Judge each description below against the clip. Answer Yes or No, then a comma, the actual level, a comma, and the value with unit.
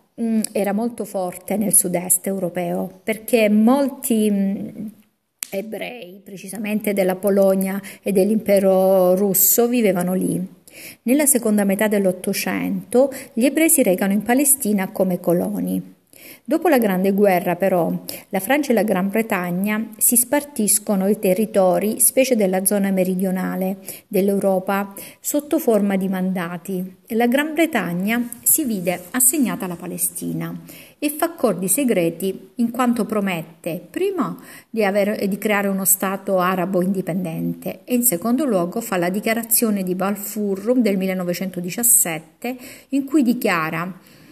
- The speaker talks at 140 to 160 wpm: No, average, 125 wpm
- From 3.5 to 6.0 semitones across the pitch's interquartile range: Yes, average, 4.0 semitones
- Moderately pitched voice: No, high, 200 Hz